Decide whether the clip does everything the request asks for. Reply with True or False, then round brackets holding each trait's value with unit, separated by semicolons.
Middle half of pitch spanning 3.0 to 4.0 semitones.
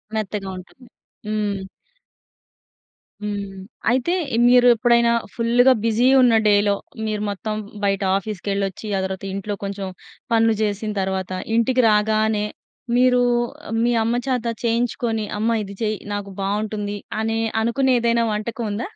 False (2.5 semitones)